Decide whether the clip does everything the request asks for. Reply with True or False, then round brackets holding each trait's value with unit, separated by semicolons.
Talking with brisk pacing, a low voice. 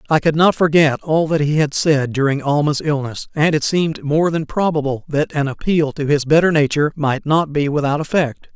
False (210 wpm; 150 Hz)